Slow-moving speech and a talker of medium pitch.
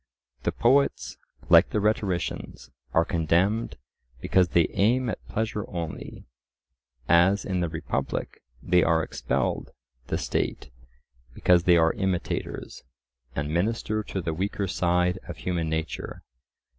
No: slow, 130 wpm; very low, 90 Hz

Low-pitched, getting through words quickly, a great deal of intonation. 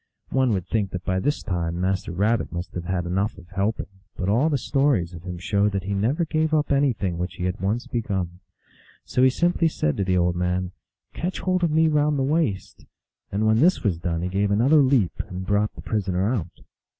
Yes: low, 100 Hz; fast, 225 wpm; wide, 6.8 semitones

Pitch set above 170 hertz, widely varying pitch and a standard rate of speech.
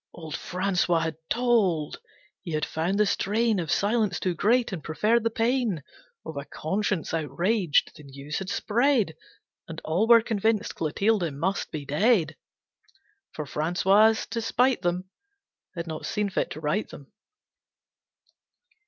Yes: high, 190 Hz; wide, 5.7 semitones; average, 145 wpm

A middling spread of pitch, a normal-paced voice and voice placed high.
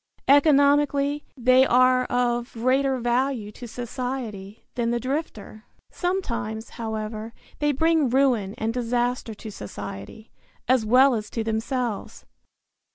No: average, 3.4 semitones; slow, 115 wpm; high, 245 Hz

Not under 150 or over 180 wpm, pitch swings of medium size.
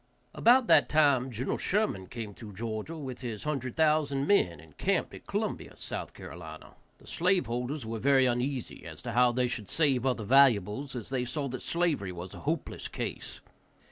Yes: average, 175 wpm; average, 4.6 semitones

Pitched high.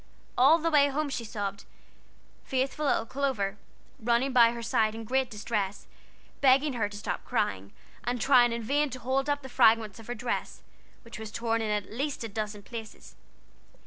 Yes: high, 235 Hz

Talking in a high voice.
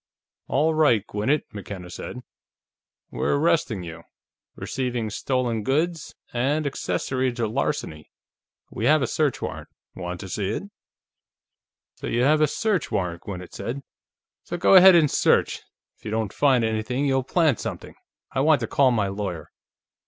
No: low, 125 Hz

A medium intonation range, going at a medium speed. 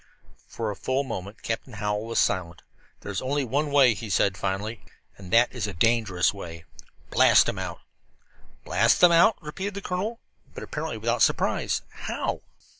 No: wide, 6.0 semitones; average, 170 wpm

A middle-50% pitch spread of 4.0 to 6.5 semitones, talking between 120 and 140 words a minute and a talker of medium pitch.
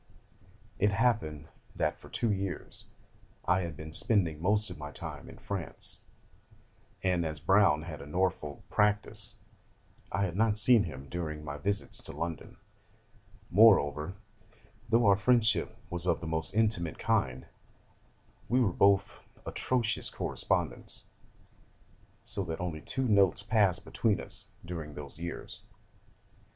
No: average, 4.8 semitones; slow, 135 wpm; very low, 90 Hz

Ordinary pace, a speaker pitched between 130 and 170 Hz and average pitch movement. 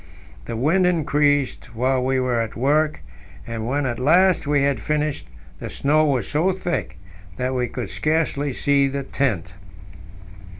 Yes: average, 155 wpm; medium, 140 Hz; average, 3.2 semitones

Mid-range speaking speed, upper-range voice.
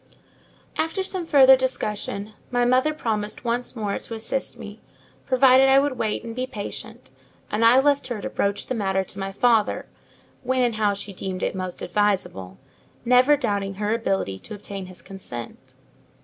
Yes: average, 170 wpm; high, 220 Hz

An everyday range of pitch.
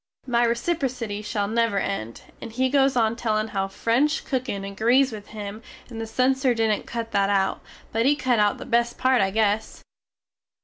Yes: average, 3.5 semitones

